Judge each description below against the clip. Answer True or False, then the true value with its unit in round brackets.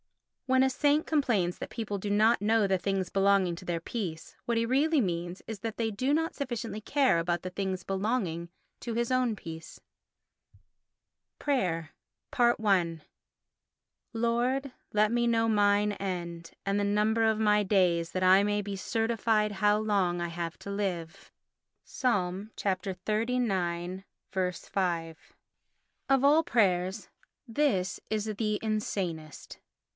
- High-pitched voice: True (205 Hz)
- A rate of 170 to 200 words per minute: False (140 wpm)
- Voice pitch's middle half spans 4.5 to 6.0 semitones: False (4.0 semitones)